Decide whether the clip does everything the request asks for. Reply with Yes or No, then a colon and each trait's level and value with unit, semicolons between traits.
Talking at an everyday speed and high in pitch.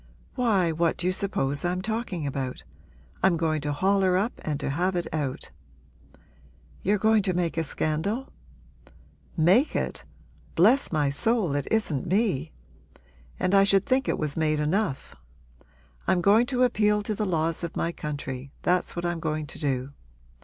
No: average, 165 wpm; medium, 175 Hz